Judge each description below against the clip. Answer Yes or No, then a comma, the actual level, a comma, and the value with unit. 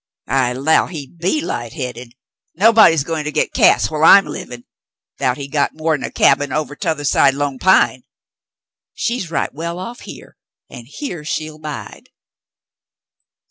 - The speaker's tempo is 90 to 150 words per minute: Yes, average, 145 wpm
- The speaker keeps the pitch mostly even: No, average, 3.6 semitones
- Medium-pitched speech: Yes, medium, 155 Hz